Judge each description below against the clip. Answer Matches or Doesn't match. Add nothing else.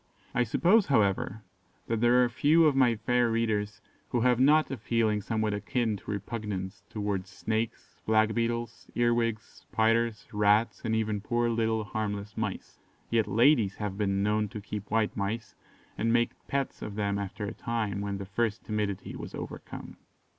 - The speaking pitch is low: Matches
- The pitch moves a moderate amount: Doesn't match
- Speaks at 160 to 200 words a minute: Matches